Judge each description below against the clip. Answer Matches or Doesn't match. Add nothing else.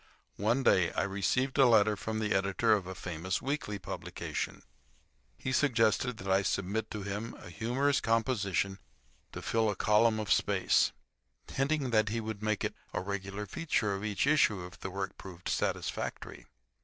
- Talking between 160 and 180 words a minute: Matches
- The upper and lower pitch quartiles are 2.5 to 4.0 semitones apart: Matches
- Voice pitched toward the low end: Matches